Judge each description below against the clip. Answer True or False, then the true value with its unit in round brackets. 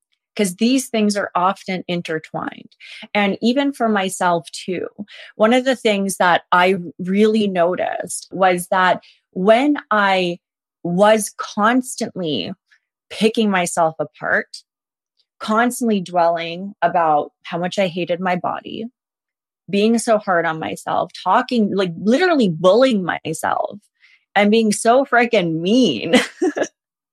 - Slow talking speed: True (115 wpm)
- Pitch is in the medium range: False (205 Hz)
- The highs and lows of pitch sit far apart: False (4.2 semitones)